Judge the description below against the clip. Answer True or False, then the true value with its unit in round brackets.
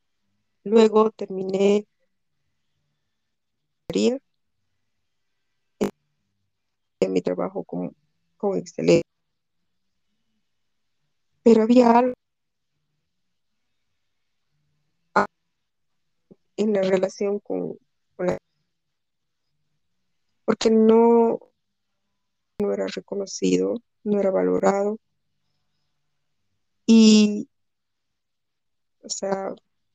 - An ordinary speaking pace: False (55 wpm)